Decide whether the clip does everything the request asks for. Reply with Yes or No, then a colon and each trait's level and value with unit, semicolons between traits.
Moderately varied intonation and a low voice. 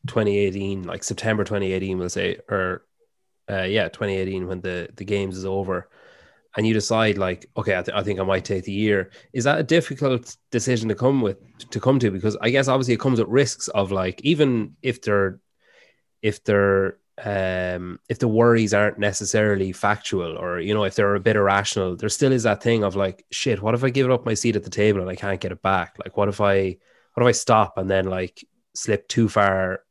Yes: average, 3.5 semitones; low, 105 Hz